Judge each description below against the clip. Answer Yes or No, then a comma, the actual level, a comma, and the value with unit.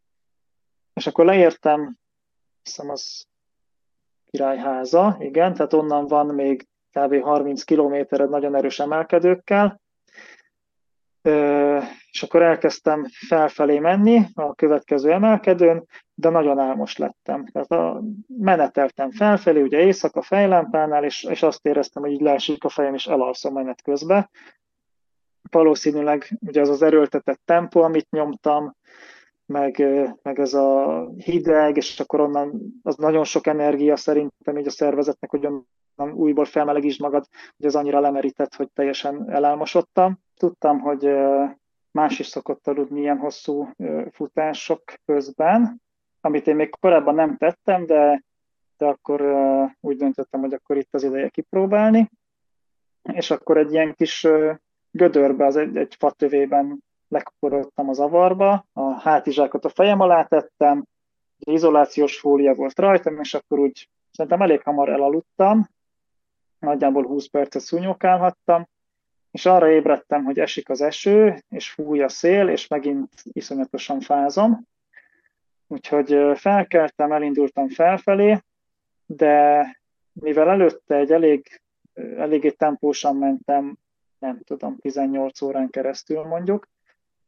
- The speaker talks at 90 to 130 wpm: Yes, average, 125 wpm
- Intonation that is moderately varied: Yes, average, 3.1 semitones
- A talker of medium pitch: Yes, medium, 150 Hz